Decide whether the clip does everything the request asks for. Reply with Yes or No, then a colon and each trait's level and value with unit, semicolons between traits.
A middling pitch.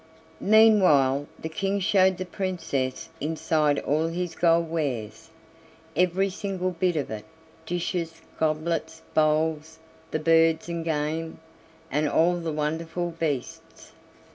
Yes: medium, 165 Hz